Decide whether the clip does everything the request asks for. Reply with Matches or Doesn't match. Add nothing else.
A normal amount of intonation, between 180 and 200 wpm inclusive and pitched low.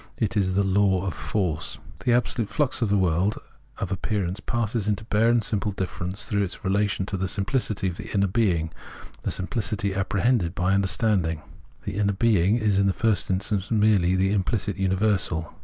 Doesn't match